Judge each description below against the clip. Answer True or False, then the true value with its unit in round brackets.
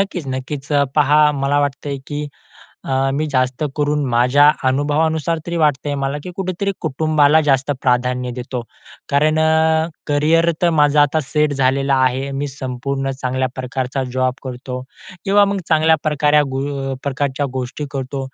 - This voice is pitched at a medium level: True (145 Hz)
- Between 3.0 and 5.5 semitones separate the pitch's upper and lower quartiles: False (2.6 semitones)